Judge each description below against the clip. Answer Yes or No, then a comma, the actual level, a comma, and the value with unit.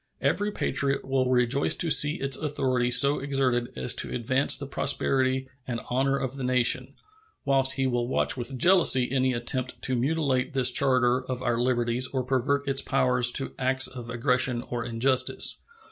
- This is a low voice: Yes, low, 130 Hz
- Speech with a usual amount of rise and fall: No, narrow, 1.7 semitones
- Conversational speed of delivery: Yes, average, 170 wpm